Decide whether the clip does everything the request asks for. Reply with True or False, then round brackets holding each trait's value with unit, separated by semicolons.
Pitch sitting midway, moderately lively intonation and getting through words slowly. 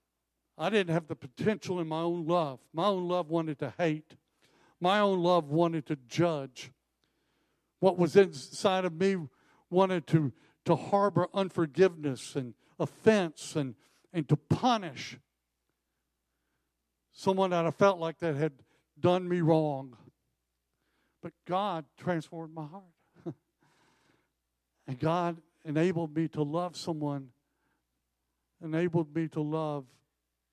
True (160 Hz; 4.7 semitones; 125 wpm)